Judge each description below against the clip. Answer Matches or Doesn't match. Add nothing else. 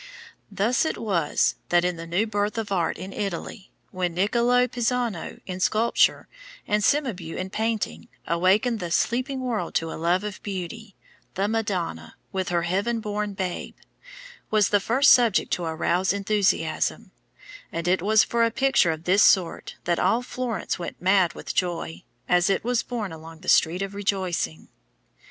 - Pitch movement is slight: Doesn't match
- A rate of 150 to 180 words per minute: Matches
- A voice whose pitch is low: Doesn't match